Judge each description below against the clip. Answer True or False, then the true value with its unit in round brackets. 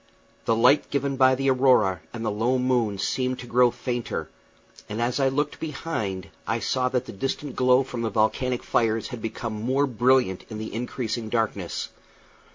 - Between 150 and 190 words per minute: True (175 wpm)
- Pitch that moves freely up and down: False (2.7 semitones)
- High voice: False (125 Hz)